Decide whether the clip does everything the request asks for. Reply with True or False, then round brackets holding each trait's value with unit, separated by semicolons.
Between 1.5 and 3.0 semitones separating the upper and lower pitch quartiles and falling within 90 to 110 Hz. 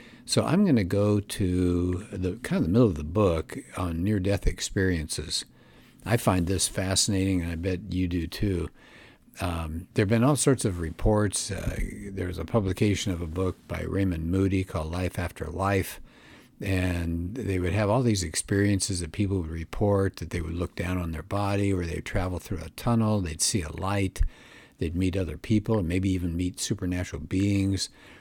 True (2.5 semitones; 95 Hz)